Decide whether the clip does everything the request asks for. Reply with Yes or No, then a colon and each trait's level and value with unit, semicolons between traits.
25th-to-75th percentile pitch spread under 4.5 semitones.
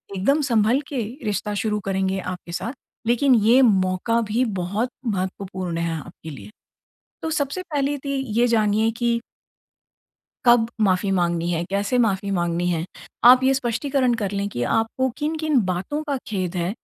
No: average, 5.2 semitones